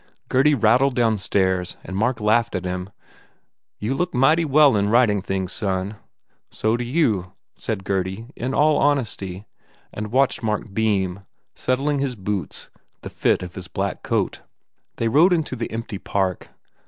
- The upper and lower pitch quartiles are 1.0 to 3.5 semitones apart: No, average, 5.2 semitones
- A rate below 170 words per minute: Yes, average, 155 wpm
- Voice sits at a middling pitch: No, low, 110 Hz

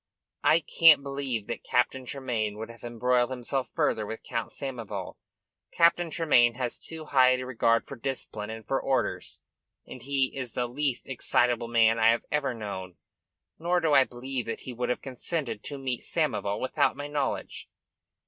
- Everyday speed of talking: Yes, average, 170 wpm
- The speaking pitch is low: Yes, low, 125 Hz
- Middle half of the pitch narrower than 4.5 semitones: Yes, average, 3.0 semitones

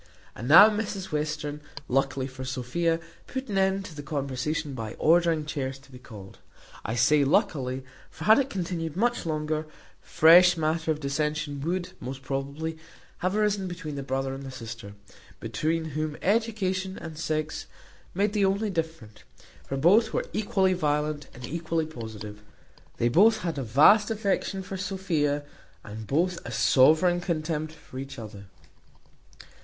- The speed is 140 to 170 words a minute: Yes, average, 150 wpm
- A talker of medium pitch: Yes, medium, 155 Hz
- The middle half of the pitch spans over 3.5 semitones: Yes, average, 5.2 semitones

